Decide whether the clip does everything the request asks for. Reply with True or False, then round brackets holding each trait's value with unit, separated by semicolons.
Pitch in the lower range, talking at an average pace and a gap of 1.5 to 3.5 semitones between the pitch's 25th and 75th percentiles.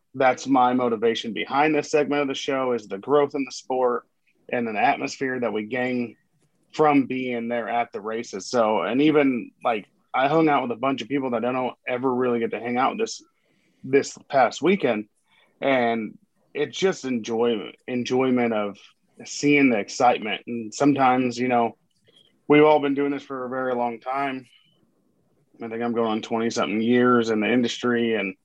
True (125 Hz; 190 wpm; 3.0 semitones)